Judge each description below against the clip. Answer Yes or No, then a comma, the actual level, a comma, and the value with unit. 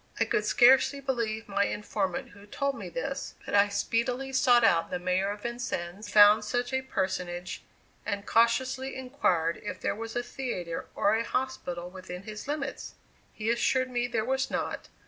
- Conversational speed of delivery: Yes, average, 170 wpm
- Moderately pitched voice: No, high, 220 Hz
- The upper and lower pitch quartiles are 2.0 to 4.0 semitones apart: No, average, 4.7 semitones